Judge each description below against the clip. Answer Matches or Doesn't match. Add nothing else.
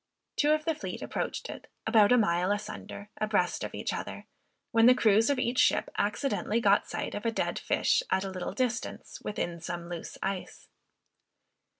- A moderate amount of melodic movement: Matches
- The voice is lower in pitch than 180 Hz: Doesn't match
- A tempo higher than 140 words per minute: Matches